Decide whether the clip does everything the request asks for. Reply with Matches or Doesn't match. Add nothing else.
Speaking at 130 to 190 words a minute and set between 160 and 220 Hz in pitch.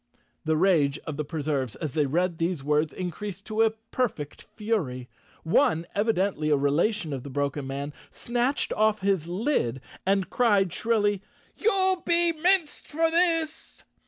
Matches